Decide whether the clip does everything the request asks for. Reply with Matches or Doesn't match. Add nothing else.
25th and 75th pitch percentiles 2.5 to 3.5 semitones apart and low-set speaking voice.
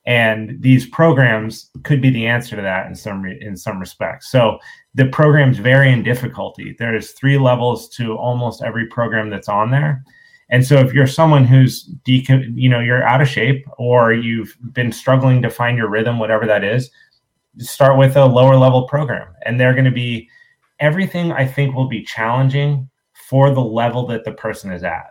Matches